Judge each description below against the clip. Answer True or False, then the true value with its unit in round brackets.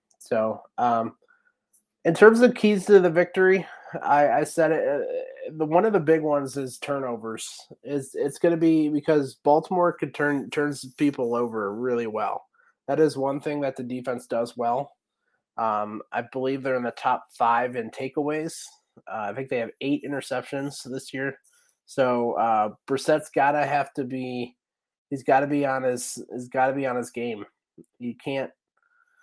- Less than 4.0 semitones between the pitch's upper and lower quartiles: False (4.5 semitones)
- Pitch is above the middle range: False (140 Hz)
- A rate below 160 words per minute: False (180 wpm)